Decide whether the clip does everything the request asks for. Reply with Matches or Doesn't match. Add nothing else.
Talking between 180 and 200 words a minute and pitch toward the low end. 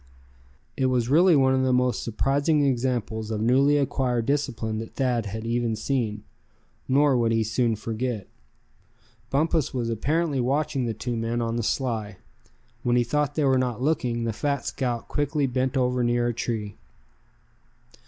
Doesn't match